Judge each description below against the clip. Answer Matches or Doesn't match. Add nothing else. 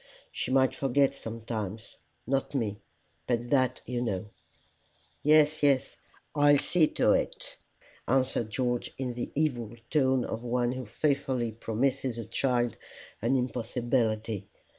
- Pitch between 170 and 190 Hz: Doesn't match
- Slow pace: Matches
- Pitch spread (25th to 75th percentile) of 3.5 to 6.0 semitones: Doesn't match